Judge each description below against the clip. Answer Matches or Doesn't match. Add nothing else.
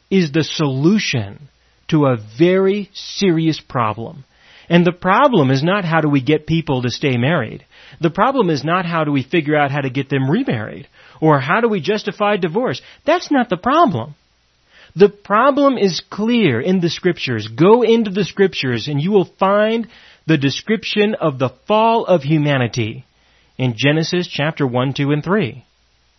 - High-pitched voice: Doesn't match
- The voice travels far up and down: Matches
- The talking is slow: Doesn't match